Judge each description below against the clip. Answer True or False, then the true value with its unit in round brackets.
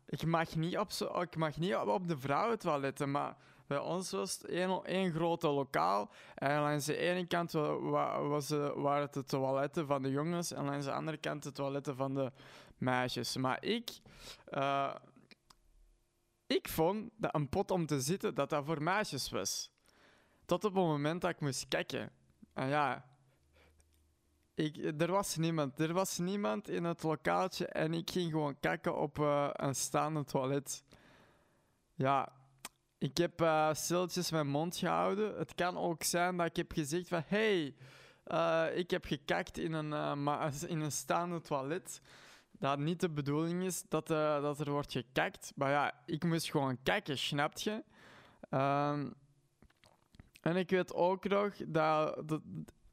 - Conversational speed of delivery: True (165 wpm)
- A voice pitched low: False (155 Hz)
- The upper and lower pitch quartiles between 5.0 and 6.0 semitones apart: False (3.5 semitones)